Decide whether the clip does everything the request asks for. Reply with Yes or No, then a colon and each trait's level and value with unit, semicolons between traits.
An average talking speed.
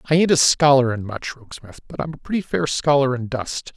No: fast, 240 wpm